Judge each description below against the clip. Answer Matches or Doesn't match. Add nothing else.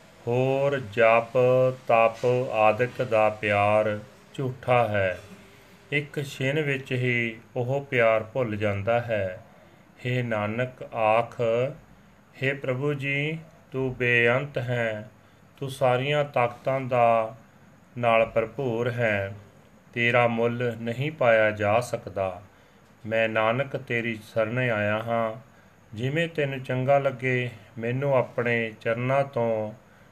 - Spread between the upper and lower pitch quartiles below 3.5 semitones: Matches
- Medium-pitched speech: Doesn't match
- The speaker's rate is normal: Matches